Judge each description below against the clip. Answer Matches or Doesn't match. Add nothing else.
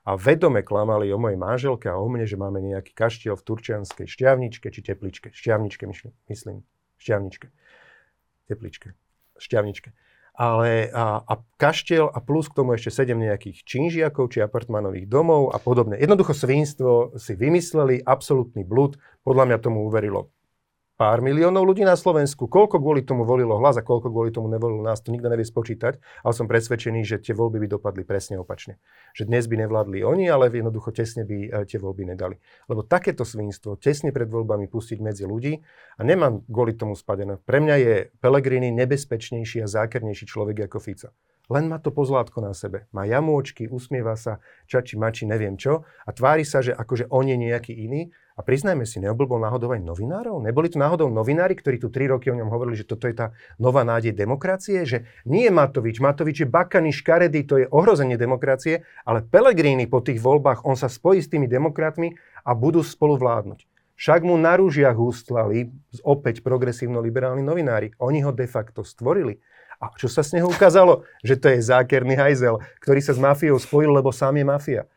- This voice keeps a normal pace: Doesn't match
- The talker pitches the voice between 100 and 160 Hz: Matches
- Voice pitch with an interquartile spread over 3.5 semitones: Matches